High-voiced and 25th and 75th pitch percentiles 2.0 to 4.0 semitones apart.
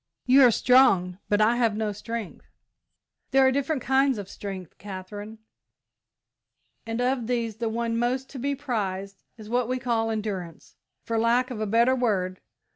Yes: high, 230 Hz; average, 3.4 semitones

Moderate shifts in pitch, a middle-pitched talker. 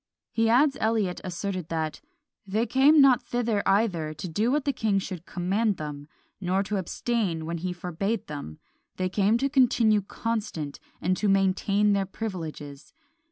No: average, 4.4 semitones; high, 195 Hz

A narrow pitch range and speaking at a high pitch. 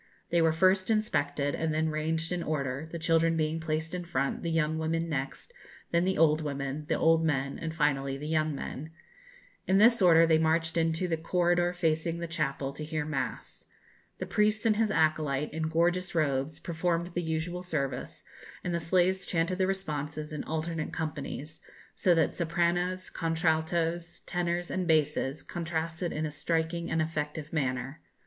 No: narrow, 2.1 semitones; medium, 160 Hz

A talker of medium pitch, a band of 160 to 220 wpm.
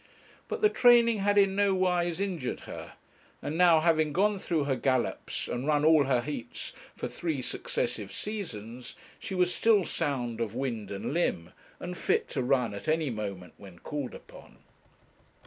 Yes: medium, 150 Hz; average, 165 wpm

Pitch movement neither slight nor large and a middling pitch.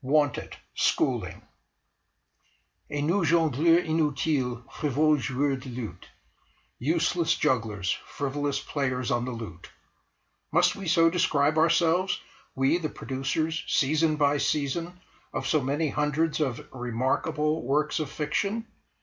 Yes: average, 3.6 semitones; medium, 150 Hz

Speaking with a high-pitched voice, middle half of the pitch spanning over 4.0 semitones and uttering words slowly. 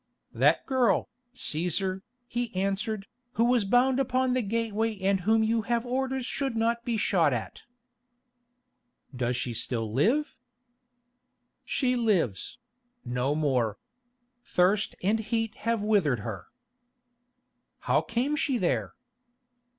Yes: high, 220 Hz; wide, 5.4 semitones; slow, 115 wpm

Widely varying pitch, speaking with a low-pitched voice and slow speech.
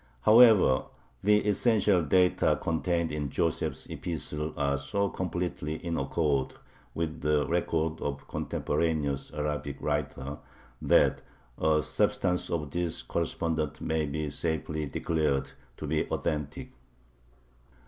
No: average, 2.9 semitones; very low, 80 Hz; slow, 110 wpm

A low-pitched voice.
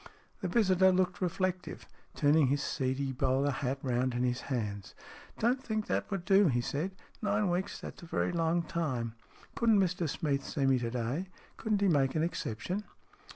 No: medium, 160 Hz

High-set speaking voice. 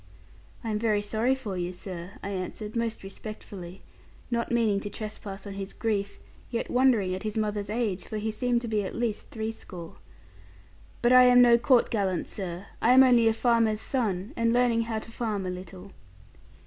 Yes: high, 215 Hz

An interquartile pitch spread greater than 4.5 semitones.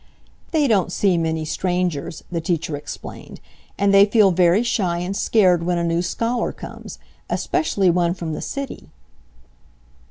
No: average, 2.9 semitones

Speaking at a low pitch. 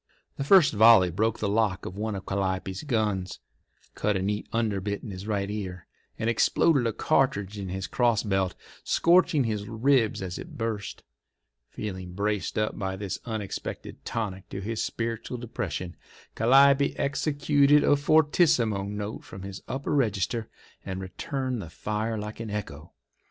Yes: low, 105 Hz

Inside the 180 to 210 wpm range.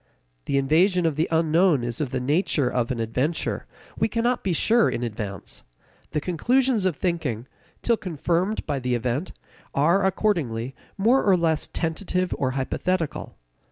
No: average, 155 wpm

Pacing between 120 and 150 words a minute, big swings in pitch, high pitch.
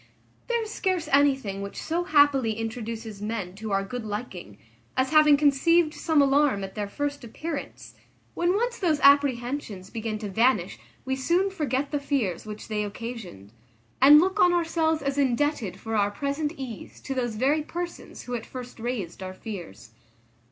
No: average, 165 wpm; wide, 5.8 semitones; very high, 260 Hz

